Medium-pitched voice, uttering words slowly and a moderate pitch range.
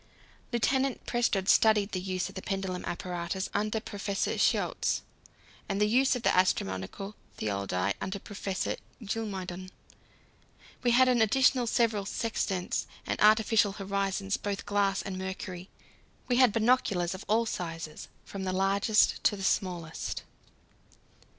No: high, 200 Hz; slow, 130 wpm; average, 3.0 semitones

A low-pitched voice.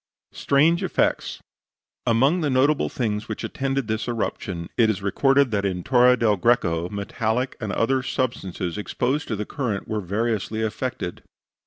Yes: low, 115 Hz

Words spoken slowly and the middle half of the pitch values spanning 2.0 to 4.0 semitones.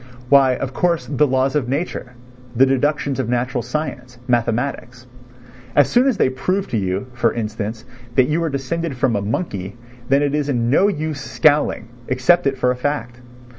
No: average, 175 wpm; average, 3.5 semitones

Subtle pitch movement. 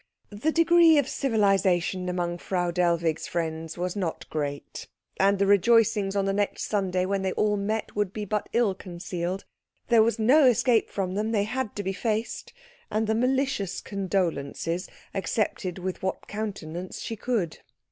No: average, 3.4 semitones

